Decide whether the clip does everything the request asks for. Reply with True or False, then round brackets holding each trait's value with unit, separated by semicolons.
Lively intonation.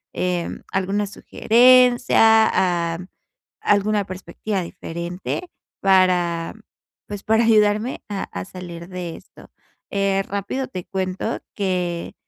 False (3.0 semitones)